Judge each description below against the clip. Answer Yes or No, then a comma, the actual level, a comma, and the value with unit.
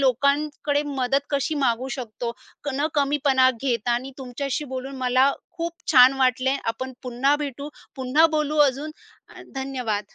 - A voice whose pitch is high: Yes, very high, 265 Hz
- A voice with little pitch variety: Yes, narrow, 2.1 semitones